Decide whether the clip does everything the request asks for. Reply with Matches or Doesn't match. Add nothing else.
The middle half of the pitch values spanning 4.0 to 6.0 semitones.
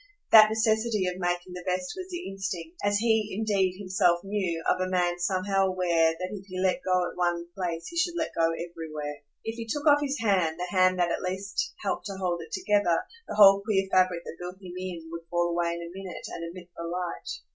Doesn't match